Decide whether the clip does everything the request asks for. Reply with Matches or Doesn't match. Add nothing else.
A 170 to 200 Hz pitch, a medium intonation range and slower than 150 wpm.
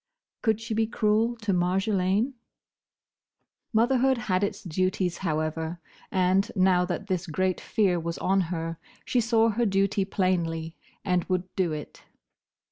Matches